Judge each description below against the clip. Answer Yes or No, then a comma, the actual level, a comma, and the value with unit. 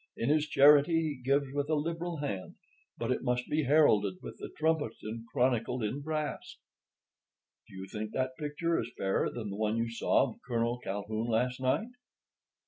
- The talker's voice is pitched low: Yes, low, 130 Hz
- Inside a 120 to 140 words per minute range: No, average, 180 wpm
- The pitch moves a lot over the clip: No, average, 4.7 semitones